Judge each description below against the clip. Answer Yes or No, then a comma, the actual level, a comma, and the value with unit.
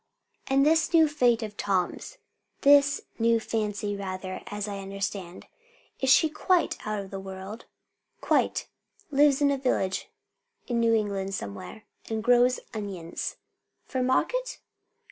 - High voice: Yes, high, 220 Hz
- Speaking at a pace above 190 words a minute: No, slow, 135 wpm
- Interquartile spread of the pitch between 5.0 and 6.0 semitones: Yes, wide, 5.6 semitones